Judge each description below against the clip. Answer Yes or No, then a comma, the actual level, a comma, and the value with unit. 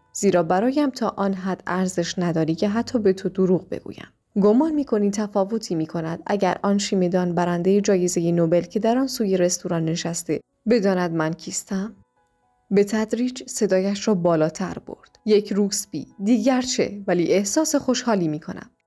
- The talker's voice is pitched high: Yes, high, 195 Hz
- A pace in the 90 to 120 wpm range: No, fast, 155 wpm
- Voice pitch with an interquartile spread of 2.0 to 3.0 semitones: No, average, 3.8 semitones